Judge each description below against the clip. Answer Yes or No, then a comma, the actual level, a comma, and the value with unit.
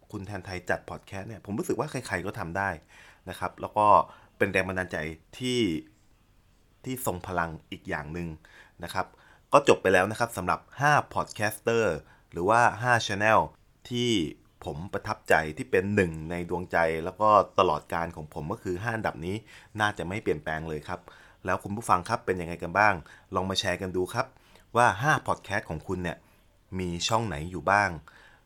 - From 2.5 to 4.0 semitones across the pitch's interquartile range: Yes, average, 3.5 semitones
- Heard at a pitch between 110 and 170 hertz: No, very low, 95 Hz